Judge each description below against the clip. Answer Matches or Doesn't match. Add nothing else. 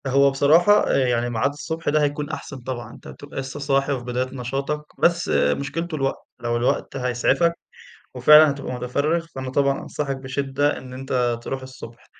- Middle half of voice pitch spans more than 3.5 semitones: Doesn't match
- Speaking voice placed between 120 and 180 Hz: Matches